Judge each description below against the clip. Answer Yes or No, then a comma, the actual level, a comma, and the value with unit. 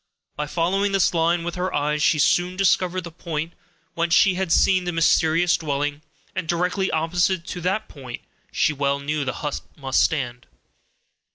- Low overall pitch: No, medium, 165 Hz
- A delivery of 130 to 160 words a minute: No, average, 170 wpm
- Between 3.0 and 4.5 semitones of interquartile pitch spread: Yes, average, 3.3 semitones